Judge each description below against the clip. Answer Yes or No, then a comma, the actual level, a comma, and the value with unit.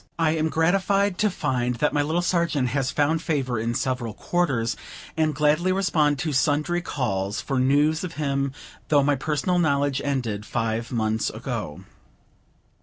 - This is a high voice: No, medium, 145 Hz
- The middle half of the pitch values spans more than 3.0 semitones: Yes, average, 4.2 semitones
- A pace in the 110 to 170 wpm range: Yes, average, 155 wpm